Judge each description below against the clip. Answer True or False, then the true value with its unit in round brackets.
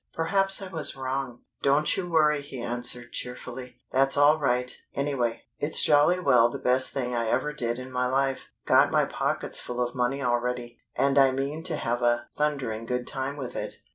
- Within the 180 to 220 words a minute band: True (190 wpm)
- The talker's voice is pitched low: True (130 Hz)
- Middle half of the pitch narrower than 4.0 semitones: True (2.8 semitones)